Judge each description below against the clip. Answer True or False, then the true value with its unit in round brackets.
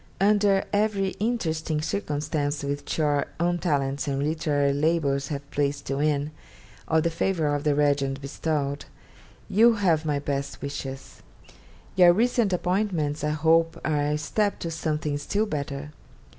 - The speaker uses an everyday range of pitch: True (3.5 semitones)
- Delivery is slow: False (145 wpm)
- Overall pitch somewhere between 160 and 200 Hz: False (150 Hz)